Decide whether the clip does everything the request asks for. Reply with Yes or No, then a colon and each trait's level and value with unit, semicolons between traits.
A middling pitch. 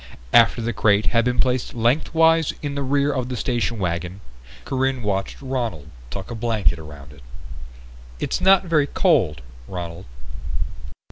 No: low, 120 Hz